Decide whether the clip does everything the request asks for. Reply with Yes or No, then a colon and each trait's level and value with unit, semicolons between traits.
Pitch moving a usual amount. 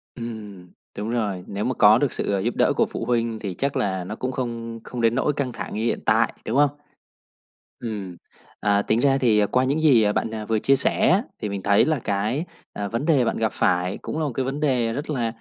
Yes: average, 4.1 semitones